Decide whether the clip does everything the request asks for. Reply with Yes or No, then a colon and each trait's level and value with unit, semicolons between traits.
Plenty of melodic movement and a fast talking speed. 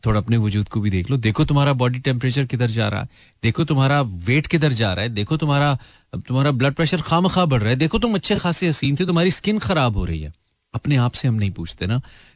Yes: wide, 6.0 semitones; fast, 250 wpm